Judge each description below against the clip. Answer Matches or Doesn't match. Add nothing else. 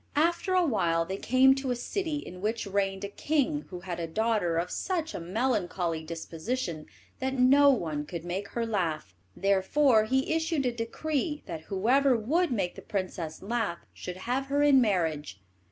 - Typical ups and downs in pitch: Doesn't match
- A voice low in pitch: Doesn't match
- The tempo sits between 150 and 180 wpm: Matches